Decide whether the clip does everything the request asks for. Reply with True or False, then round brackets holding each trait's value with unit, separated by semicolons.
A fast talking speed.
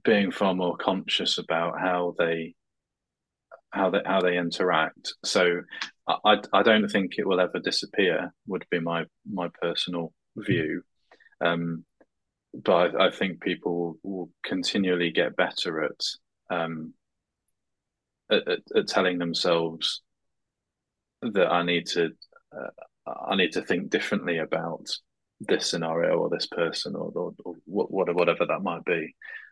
False (135 wpm)